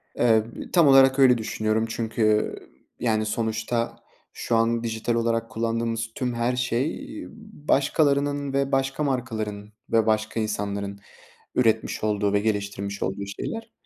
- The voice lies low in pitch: Yes, low, 115 Hz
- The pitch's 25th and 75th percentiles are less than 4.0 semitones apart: Yes, average, 2.9 semitones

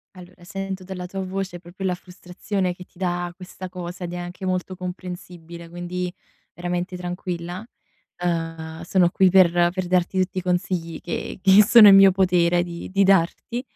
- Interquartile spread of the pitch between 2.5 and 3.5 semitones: No, narrow, 1.3 semitones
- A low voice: No, medium, 180 Hz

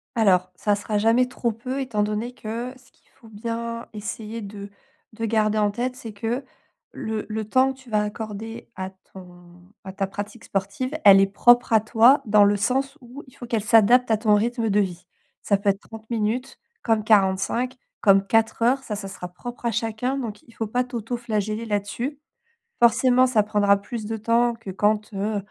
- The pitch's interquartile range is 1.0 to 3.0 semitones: Yes, narrow, 2.6 semitones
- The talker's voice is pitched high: Yes, high, 220 Hz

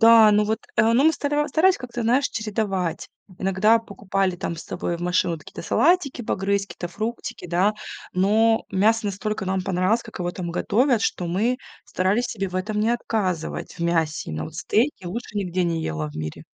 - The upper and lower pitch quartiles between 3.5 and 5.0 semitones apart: Yes, average, 4.1 semitones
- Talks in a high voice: Yes, high, 200 Hz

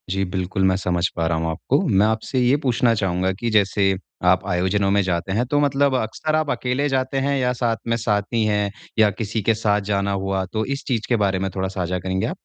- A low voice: Yes, low, 105 Hz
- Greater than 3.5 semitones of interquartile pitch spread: Yes, average, 4.2 semitones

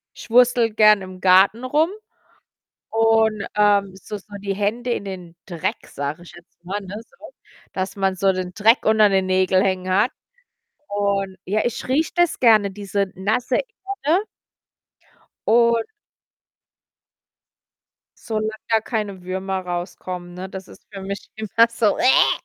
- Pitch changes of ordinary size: Yes, average, 3.1 semitones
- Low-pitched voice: No, high, 200 Hz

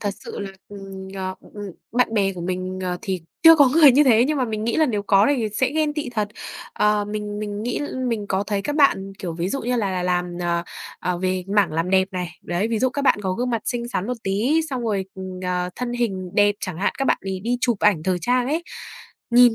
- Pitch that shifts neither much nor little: Yes, average, 4.6 semitones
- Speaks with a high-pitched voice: Yes, high, 205 Hz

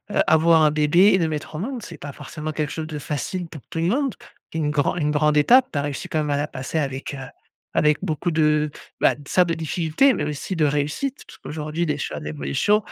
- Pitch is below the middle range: No, medium, 155 Hz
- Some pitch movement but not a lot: No, narrow, 2.2 semitones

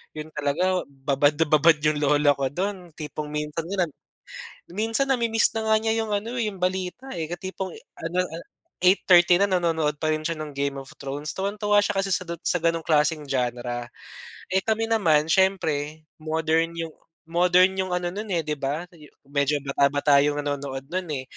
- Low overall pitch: No, medium, 165 Hz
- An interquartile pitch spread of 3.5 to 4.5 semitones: Yes, average, 4.2 semitones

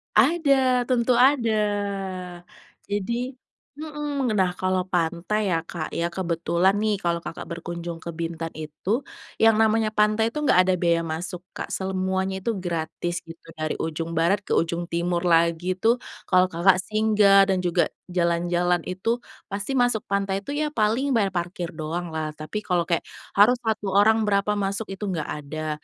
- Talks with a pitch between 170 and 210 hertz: Yes, medium, 185 Hz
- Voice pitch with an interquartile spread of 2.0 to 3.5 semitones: No, average, 4.2 semitones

